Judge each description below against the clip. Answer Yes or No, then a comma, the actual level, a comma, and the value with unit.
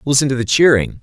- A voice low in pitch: Yes, low, 130 Hz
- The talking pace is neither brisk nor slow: No, fast, 235 wpm